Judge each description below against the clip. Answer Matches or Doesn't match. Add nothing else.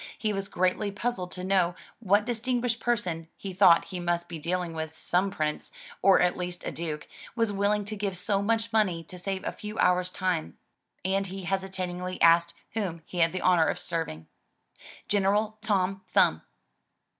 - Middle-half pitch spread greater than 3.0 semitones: Doesn't match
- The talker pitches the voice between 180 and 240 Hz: Matches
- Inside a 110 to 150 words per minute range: Doesn't match